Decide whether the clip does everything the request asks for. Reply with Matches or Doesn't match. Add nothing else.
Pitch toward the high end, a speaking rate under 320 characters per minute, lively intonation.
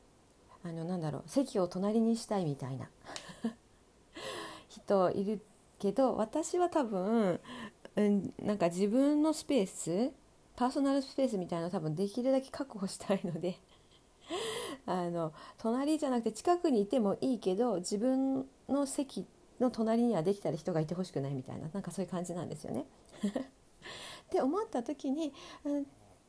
Matches